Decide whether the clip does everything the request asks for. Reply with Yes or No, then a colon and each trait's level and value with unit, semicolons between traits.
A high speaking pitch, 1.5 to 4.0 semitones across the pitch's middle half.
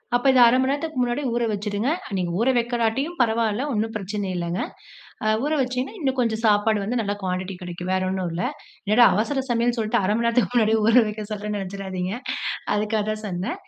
Yes: high, 220 Hz; average, 3.4 semitones